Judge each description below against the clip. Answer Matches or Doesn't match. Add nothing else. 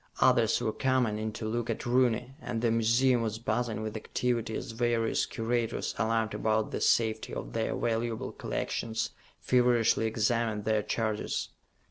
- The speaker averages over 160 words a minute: Doesn't match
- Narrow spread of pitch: Matches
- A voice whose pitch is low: Matches